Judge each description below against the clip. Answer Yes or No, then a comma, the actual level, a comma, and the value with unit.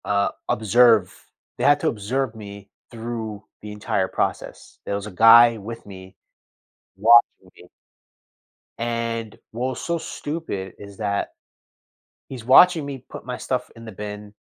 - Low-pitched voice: Yes, low, 115 Hz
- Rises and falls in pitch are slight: No, average, 3.4 semitones